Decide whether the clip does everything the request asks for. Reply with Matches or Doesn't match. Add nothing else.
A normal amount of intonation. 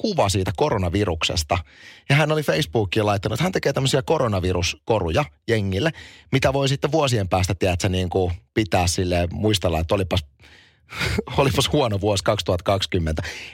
Matches